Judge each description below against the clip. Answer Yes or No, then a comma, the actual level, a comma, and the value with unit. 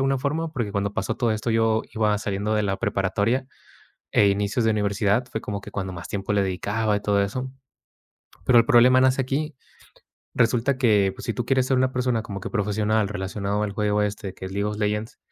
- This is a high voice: No, low, 105 Hz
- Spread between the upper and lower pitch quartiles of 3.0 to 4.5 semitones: Yes, average, 3.3 semitones